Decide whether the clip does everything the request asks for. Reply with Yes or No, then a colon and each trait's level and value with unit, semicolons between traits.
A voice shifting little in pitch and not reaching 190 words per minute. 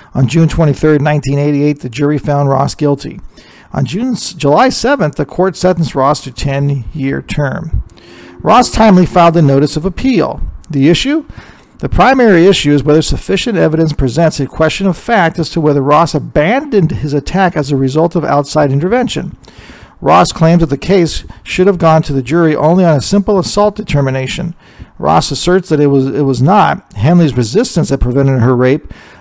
No: average, 4.4 semitones; average, 175 wpm